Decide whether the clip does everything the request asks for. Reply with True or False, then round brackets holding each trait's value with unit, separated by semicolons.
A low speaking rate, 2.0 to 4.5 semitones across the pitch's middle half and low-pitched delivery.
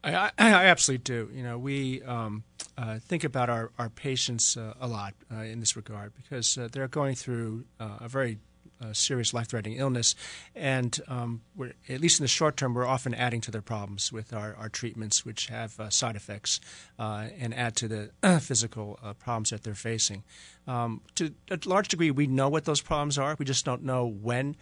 False (205 wpm; 3.3 semitones; 120 Hz)